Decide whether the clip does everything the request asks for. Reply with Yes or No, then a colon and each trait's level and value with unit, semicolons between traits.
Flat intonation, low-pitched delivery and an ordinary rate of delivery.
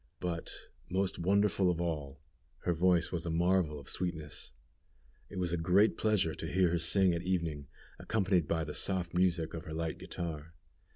Yes: narrow, 2.3 semitones; very low, 85 Hz; average, 175 wpm